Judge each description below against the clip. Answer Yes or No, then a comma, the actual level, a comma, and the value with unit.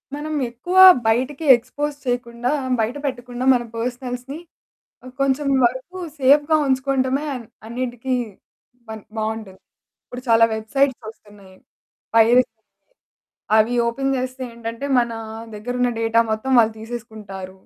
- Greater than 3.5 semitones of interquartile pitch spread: No, average, 2.7 semitones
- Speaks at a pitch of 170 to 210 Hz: No, high, 245 Hz